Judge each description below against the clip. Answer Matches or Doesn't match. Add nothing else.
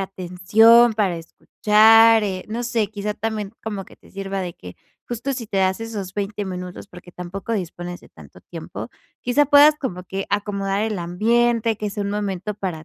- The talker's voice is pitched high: Matches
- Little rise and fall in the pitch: Doesn't match